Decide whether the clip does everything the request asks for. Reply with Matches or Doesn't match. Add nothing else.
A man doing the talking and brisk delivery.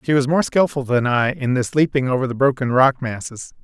Matches